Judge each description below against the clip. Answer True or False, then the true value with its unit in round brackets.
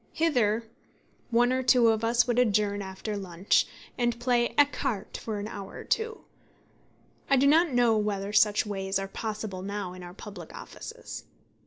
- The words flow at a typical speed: True (165 wpm)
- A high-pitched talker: True (215 Hz)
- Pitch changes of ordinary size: True (3.6 semitones)